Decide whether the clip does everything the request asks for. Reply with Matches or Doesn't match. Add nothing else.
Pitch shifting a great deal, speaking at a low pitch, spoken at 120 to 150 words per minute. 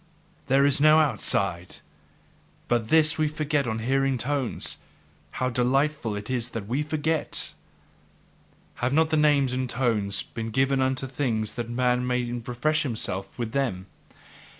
Doesn't match